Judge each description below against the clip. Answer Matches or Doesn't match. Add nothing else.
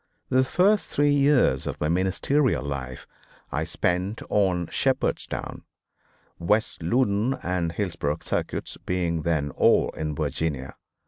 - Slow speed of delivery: Matches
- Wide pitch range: Matches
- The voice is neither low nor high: Doesn't match